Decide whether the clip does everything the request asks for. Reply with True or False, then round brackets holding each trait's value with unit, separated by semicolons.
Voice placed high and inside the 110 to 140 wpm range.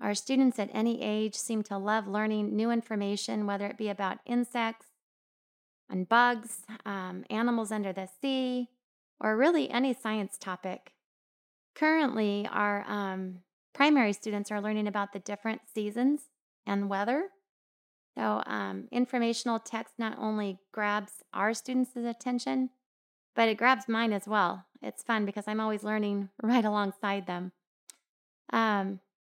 True (215 Hz; 135 wpm)